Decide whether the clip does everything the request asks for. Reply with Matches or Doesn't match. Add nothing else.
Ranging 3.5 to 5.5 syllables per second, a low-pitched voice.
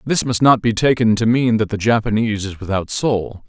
Matches